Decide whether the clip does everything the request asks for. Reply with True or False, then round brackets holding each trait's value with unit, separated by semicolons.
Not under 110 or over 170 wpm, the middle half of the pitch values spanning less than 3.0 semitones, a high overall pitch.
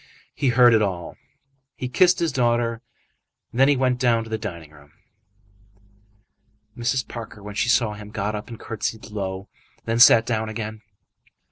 False (160 wpm; 2.4 semitones; 115 Hz)